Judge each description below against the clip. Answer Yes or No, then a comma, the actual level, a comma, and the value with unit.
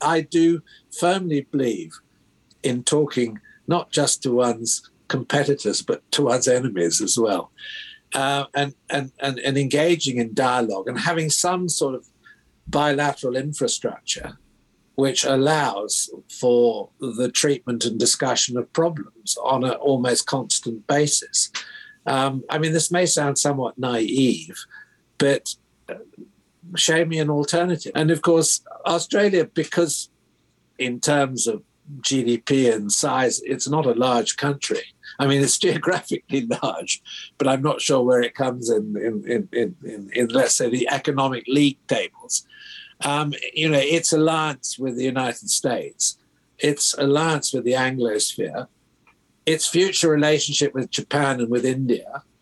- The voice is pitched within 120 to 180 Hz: Yes, medium, 140 Hz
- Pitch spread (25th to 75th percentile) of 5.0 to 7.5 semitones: No, average, 4.0 semitones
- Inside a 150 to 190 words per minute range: No, average, 140 wpm